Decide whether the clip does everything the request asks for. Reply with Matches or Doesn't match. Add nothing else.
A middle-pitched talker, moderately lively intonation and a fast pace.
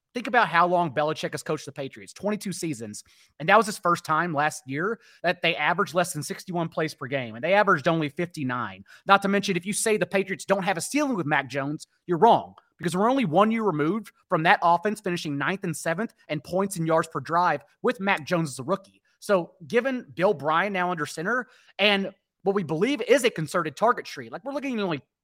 Matches